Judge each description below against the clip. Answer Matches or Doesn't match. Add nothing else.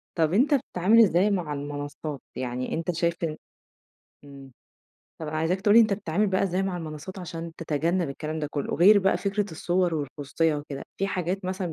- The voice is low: Doesn't match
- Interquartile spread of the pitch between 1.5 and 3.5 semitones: Doesn't match